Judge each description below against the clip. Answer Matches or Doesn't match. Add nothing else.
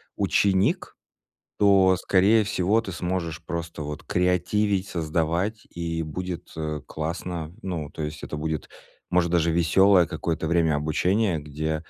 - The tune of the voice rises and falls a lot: Doesn't match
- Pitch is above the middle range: Doesn't match